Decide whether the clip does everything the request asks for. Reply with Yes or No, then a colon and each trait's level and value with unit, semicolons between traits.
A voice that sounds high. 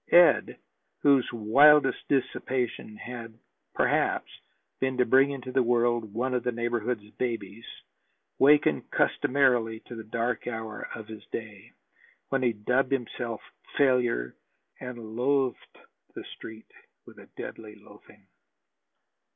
No: low, 120 Hz